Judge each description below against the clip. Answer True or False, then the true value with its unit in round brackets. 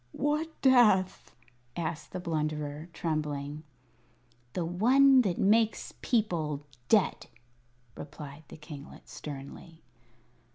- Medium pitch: True (165 Hz)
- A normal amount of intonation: False (6.5 semitones)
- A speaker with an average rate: False (90 wpm)